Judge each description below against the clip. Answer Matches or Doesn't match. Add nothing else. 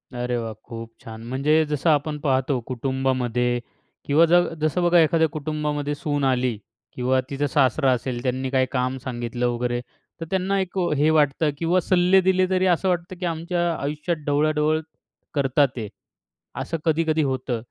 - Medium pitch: Matches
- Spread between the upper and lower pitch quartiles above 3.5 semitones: Matches